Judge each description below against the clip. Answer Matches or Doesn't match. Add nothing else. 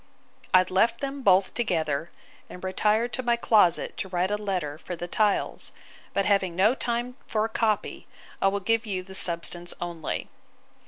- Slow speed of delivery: Doesn't match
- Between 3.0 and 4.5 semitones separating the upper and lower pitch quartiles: Matches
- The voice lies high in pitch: Matches